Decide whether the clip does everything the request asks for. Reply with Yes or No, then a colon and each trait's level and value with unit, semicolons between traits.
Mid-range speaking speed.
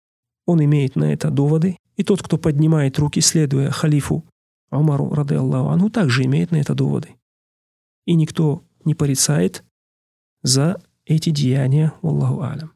Yes: average, 145 wpm